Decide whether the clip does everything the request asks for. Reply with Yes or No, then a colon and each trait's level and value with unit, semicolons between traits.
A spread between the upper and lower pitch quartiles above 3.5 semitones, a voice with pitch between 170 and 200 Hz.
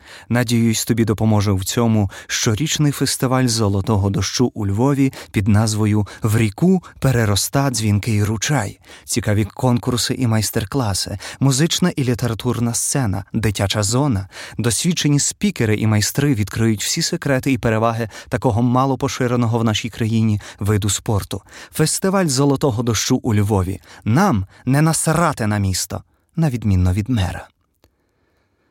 No: average, 4.2 semitones; low, 115 Hz